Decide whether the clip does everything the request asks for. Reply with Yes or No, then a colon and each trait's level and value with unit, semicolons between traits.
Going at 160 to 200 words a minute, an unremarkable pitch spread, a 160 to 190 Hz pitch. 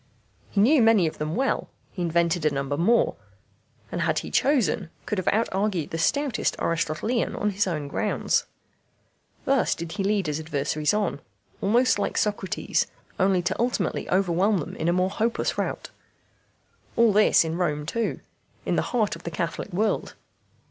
Yes: average, 170 wpm; average, 4.8 semitones; medium, 185 Hz